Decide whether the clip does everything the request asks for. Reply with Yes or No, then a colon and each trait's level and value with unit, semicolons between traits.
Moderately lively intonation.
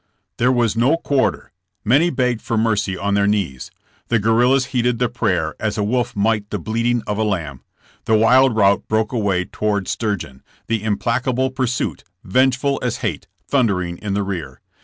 Yes: average, 3.6 semitones